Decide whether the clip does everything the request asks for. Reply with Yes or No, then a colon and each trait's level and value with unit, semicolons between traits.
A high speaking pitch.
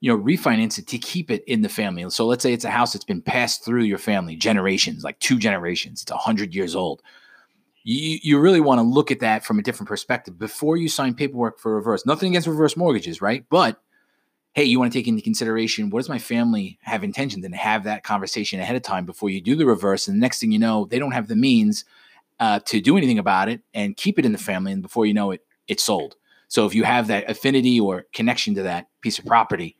No: medium, 140 Hz